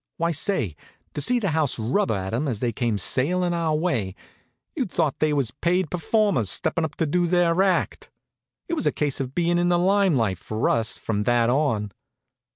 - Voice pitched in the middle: Yes, medium, 155 Hz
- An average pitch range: No, wide, 7.0 semitones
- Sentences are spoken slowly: No, average, 200 wpm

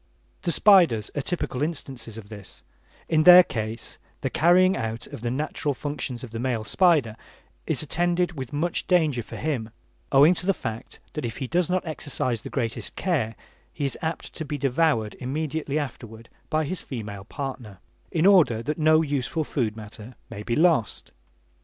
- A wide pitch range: Yes, wide, 5.8 semitones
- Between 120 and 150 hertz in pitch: Yes, medium, 140 Hz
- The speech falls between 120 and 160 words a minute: No, average, 175 wpm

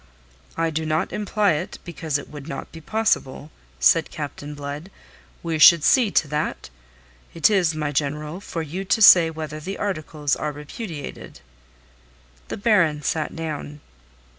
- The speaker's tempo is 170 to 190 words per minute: No, average, 150 wpm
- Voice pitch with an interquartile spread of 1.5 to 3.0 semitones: Yes, average, 2.7 semitones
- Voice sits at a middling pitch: Yes, medium, 155 Hz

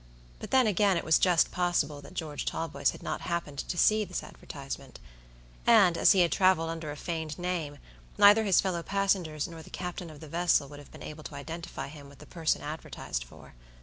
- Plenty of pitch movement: No, average, 3.5 semitones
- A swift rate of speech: Yes, fast, 210 wpm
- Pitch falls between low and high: Yes, medium, 165 Hz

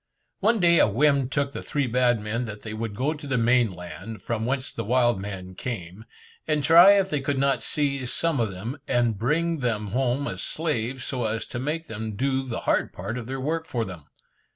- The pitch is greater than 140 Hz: No, low, 125 Hz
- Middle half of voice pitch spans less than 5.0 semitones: Yes, average, 4.4 semitones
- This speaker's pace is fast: Yes, fast, 220 wpm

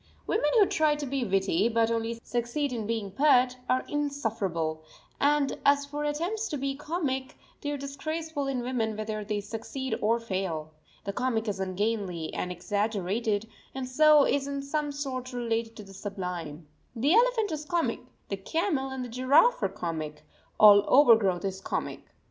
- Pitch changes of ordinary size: No, wide, 5.8 semitones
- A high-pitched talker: Yes, high, 245 Hz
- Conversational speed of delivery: Yes, average, 165 wpm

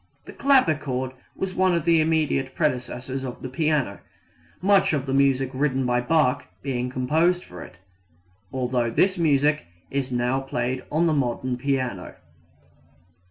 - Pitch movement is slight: No, average, 3.7 semitones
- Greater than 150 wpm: No, average, 145 wpm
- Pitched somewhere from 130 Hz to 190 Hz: Yes, low, 135 Hz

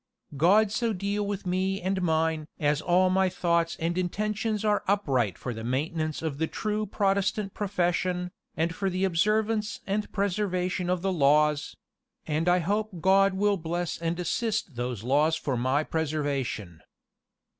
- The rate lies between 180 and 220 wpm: No, average, 155 wpm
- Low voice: No, medium, 180 Hz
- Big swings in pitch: No, average, 4.2 semitones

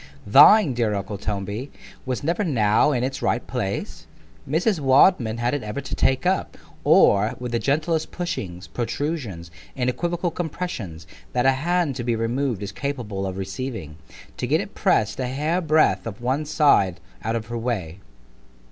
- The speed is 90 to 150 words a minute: No, average, 160 wpm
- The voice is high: No, low, 125 Hz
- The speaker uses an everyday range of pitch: No, wide, 6.0 semitones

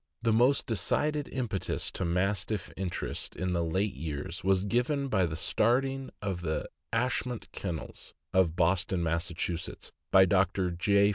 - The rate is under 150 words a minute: Yes, slow, 135 wpm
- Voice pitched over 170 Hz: No, very low, 95 Hz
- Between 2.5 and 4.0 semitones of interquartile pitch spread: No, average, 4.7 semitones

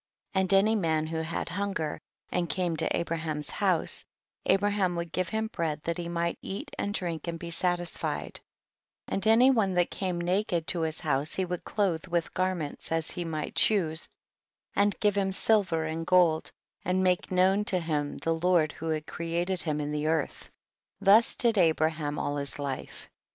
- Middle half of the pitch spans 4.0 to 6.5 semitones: No, average, 3.1 semitones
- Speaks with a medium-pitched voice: Yes, medium, 170 Hz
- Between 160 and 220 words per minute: Yes, average, 180 wpm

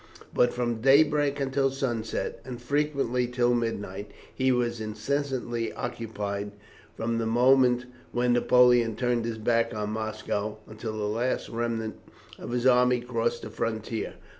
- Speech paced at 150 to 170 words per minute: No, average, 140 wpm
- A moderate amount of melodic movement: No, narrow, 2.1 semitones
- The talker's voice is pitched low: Yes, low, 120 Hz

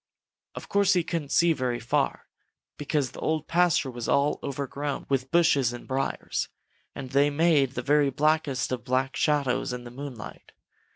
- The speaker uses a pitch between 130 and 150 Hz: Yes, medium, 140 Hz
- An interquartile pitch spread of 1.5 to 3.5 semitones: Yes, average, 3.0 semitones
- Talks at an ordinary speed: Yes, average, 165 wpm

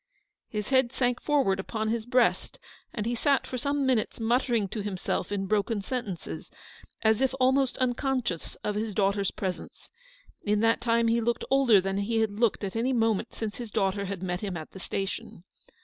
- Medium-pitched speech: No, high, 220 Hz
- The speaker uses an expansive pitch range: No, average, 3.7 semitones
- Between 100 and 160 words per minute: No, average, 185 wpm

